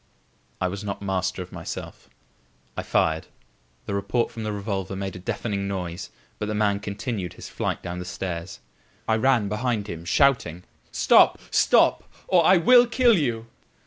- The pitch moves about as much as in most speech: Yes, average, 4.0 semitones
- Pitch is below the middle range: Yes, low, 100 Hz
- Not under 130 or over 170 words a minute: Yes, average, 165 wpm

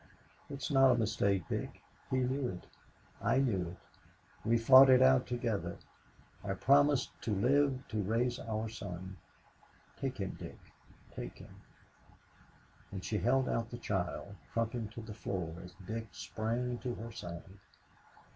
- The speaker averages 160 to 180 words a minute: No, average, 150 wpm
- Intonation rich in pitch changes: No, average, 4.2 semitones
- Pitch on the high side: No, low, 115 Hz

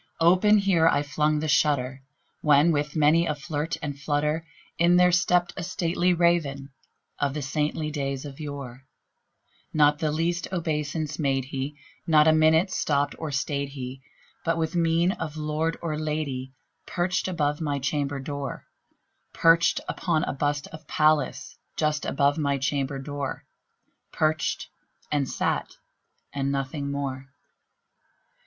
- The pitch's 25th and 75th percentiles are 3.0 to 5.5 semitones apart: No, narrow, 2.5 semitones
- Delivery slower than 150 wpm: Yes, average, 140 wpm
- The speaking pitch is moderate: Yes, medium, 150 Hz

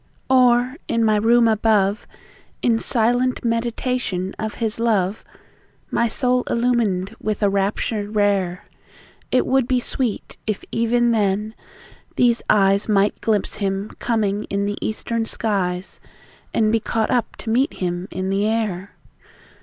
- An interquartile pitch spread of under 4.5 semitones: Yes, average, 2.8 semitones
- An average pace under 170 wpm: Yes, average, 140 wpm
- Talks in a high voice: Yes, high, 220 Hz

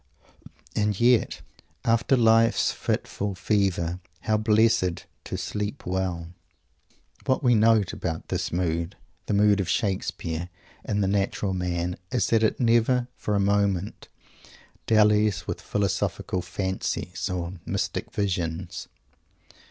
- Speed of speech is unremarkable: No, slow, 120 wpm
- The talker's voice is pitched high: No, low, 100 Hz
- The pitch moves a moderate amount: Yes, average, 3.1 semitones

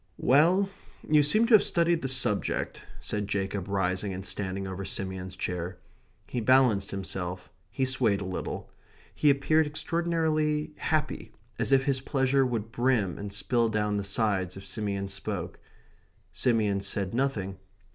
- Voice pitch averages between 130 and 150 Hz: No, low, 110 Hz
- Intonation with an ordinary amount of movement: No, wide, 6.0 semitones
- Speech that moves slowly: No, average, 145 wpm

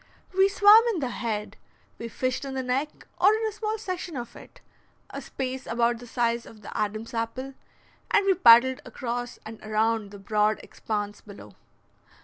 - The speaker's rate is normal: Yes, average, 175 wpm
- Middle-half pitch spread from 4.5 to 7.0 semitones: Yes, average, 5.1 semitones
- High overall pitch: Yes, high, 240 Hz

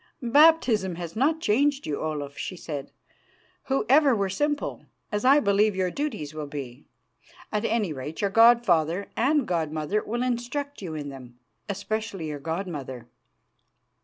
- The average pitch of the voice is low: No, high, 200 Hz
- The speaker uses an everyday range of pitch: No, wide, 7.7 semitones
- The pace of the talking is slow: No, average, 160 wpm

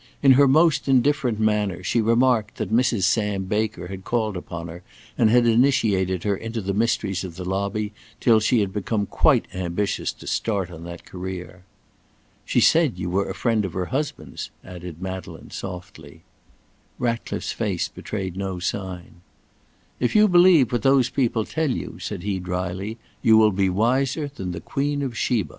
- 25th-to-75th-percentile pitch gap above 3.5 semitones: Yes, average, 4.5 semitones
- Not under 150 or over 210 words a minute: Yes, average, 170 wpm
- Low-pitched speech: Yes, low, 105 Hz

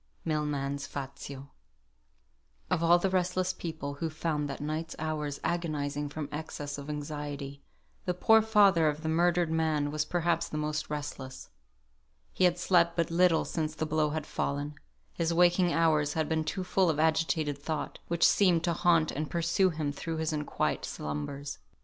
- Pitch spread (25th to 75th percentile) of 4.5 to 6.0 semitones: No, narrow, 2.5 semitones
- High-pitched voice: No, medium, 155 Hz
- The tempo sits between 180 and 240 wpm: No, average, 165 wpm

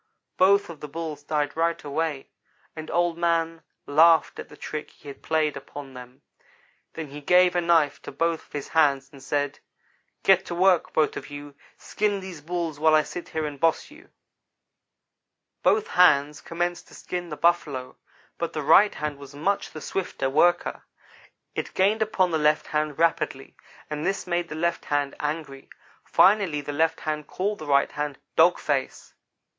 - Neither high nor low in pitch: Yes, medium, 160 Hz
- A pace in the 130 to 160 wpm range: No, average, 175 wpm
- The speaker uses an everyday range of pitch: Yes, average, 3.0 semitones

